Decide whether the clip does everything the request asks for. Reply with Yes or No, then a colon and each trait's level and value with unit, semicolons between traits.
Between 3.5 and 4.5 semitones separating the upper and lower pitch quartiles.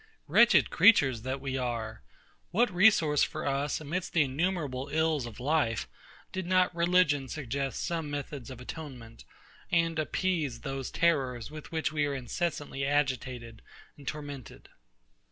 Yes: average, 3.9 semitones